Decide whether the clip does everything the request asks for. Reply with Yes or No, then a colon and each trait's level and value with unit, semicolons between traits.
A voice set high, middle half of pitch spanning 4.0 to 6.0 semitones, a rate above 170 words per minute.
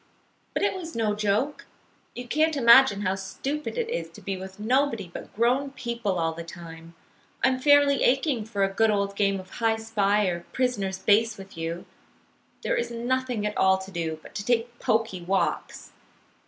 Yes: high, 215 Hz; average, 5.0 semitones; average, 180 wpm